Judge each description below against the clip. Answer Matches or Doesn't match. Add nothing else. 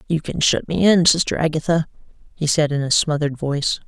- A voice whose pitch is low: Doesn't match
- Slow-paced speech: Doesn't match